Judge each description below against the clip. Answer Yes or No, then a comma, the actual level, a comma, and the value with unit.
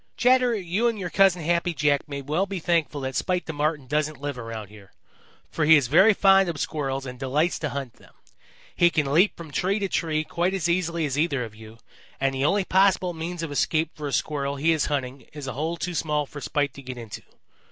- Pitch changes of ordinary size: Yes, average, 4.1 semitones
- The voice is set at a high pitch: No, medium, 155 Hz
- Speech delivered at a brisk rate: Yes, fast, 230 wpm